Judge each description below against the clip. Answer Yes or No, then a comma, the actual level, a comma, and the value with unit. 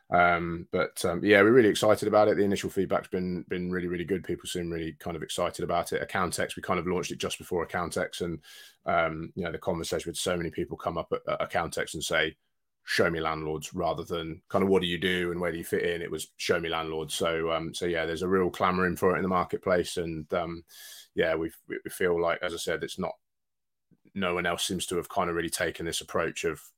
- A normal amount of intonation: No, narrow, 1.8 semitones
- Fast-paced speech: Yes, fast, 250 wpm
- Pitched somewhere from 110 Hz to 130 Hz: No, very low, 85 Hz